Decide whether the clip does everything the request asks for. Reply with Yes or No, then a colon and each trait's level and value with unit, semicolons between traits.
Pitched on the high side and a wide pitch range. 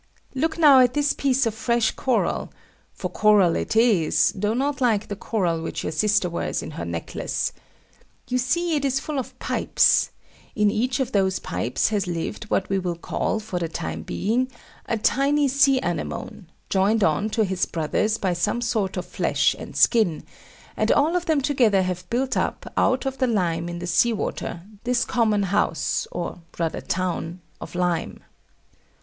Yes: high, 215 Hz; wide, 6.1 semitones